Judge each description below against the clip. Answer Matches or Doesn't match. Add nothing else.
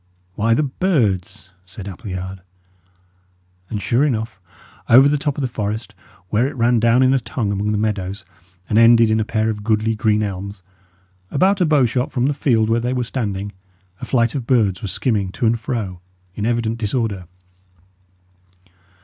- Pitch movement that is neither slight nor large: Matches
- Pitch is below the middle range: Matches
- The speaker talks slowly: Doesn't match